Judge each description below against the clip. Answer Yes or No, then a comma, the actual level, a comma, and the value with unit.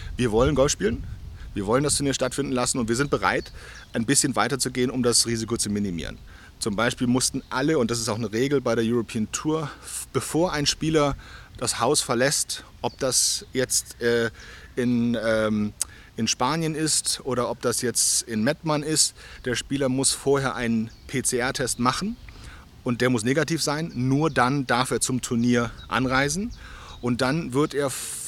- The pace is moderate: Yes, average, 170 wpm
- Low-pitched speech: Yes, low, 125 Hz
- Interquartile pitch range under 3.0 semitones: No, average, 3.4 semitones